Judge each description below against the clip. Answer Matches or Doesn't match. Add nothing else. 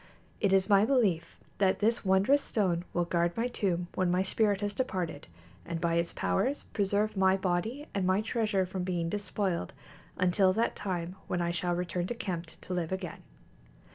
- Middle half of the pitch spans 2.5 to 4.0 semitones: Matches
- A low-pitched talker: Doesn't match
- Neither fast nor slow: Matches